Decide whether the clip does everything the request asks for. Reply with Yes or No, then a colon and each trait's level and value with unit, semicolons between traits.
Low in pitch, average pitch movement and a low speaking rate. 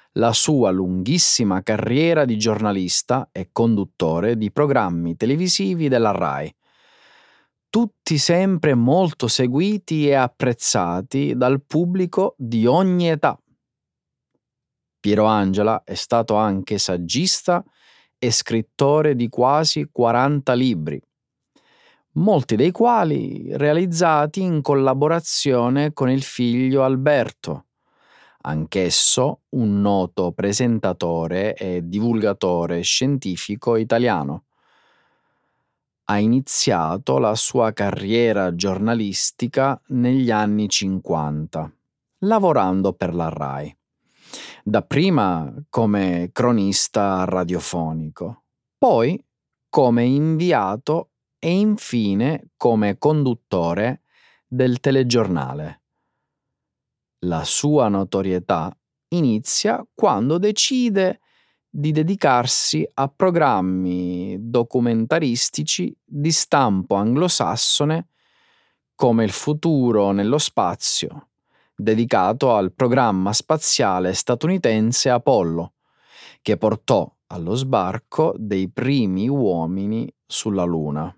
No: low, 120 Hz; wide, 7.0 semitones; slow, 85 wpm